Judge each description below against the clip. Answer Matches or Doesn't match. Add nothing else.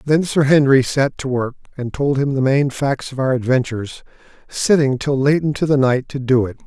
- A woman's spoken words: Doesn't match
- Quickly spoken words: Matches